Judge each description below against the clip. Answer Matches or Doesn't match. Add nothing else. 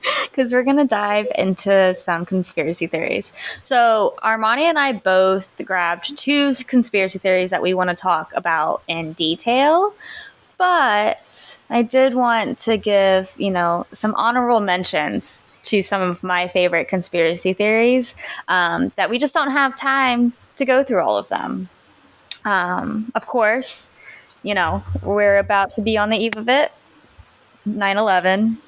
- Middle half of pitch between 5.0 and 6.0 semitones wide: Matches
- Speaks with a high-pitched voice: Matches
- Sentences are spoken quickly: Doesn't match